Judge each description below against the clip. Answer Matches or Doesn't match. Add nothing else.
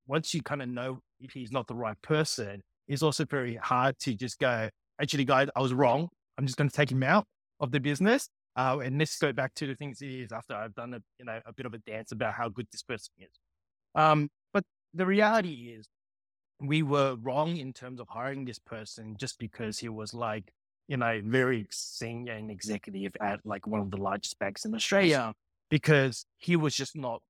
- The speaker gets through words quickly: Matches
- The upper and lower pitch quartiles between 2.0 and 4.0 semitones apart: Doesn't match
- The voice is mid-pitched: Doesn't match